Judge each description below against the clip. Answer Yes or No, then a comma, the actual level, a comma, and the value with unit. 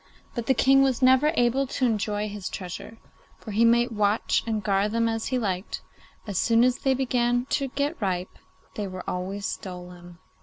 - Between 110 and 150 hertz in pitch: No, high, 225 Hz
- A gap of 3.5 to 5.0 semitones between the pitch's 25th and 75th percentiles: Yes, average, 4.1 semitones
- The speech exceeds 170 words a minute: Yes, average, 185 wpm